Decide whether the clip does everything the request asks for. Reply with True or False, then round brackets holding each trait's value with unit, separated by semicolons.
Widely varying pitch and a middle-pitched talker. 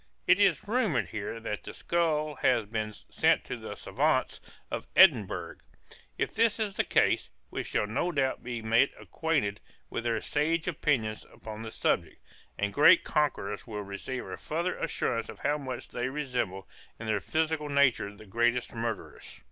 False (6.0 semitones; 125 Hz)